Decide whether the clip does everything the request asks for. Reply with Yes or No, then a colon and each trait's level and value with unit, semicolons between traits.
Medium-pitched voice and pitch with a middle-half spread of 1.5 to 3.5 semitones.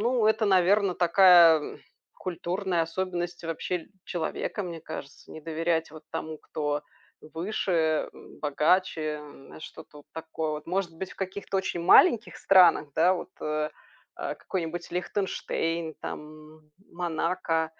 Yes: medium, 170 Hz; average, 2.8 semitones